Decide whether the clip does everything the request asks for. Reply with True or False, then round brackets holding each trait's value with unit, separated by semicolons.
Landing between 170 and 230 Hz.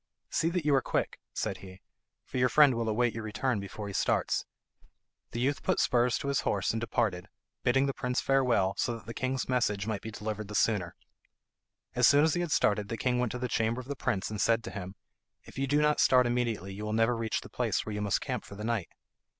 False (115 Hz)